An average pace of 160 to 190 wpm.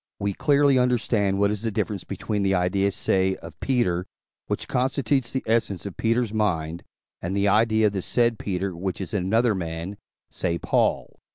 Yes: average, 180 wpm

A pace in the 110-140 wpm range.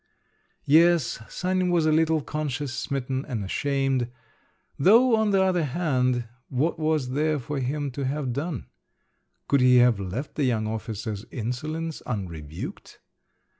Yes: slow, 135 wpm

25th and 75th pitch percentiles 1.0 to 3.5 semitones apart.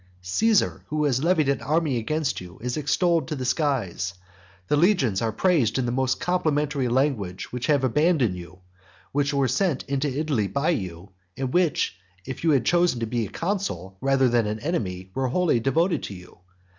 No: average, 5.3 semitones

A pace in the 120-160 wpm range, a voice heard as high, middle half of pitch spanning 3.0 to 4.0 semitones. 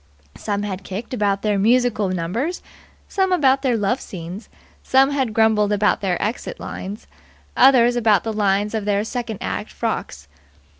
Yes: average, 155 wpm; high, 215 Hz; average, 3.5 semitones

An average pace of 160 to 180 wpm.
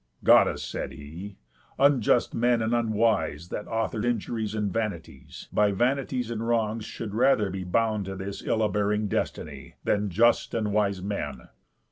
No: average, 150 wpm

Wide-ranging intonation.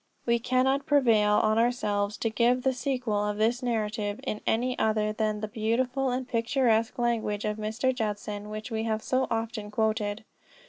No: average, 2.7 semitones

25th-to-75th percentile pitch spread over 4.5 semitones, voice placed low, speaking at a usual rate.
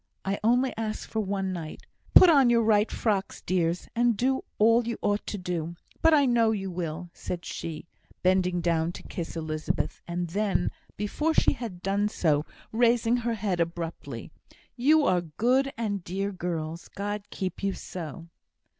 No: average, 5.0 semitones; high, 195 Hz; average, 165 wpm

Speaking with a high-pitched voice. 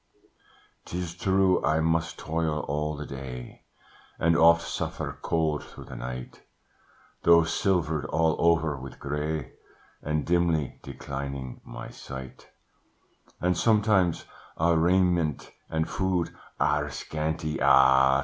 No: very low, 80 Hz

